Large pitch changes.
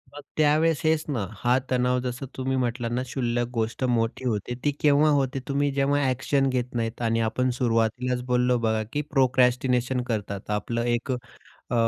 No: narrow, 2.5 semitones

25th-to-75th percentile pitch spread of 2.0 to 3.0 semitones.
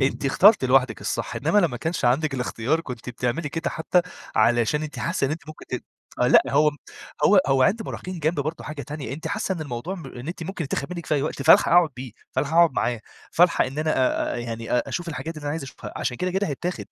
No: average, 4.3 semitones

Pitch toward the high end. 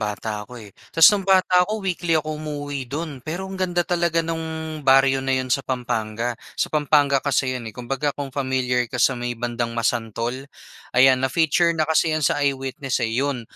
No: low, 135 Hz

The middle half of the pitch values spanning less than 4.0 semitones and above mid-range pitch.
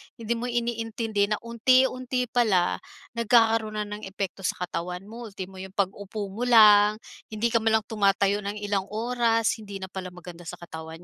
Yes: average, 3.0 semitones; high, 210 Hz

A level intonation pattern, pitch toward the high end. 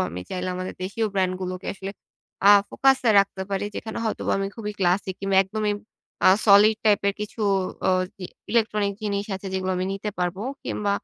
Yes: narrow, 2.0 semitones; high, 200 Hz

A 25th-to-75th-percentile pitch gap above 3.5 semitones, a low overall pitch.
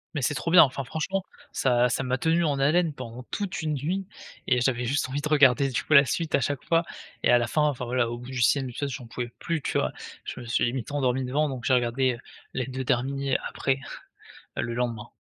No: average, 3.0 semitones; low, 130 Hz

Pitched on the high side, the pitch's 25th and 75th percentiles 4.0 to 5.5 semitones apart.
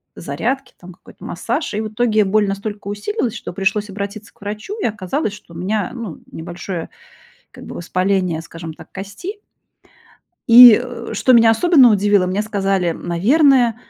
No: high, 205 Hz; average, 3.6 semitones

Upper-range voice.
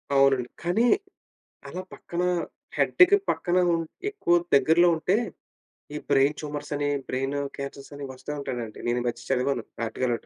No: medium, 140 Hz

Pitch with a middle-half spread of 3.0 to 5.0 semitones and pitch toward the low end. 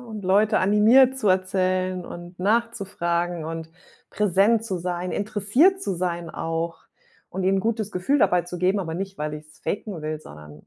No: average, 3.4 semitones; medium, 185 Hz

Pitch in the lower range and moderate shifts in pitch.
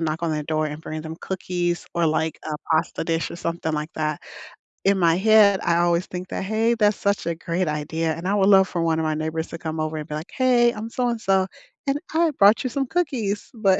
No: medium, 175 Hz; average, 4.5 semitones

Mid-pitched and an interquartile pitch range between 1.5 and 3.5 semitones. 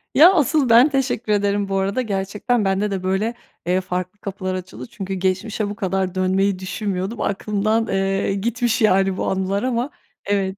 No: high, 200 Hz; average, 2.8 semitones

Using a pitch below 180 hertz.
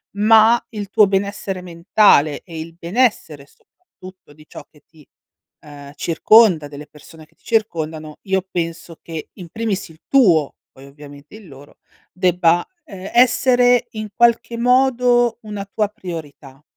No: medium, 185 Hz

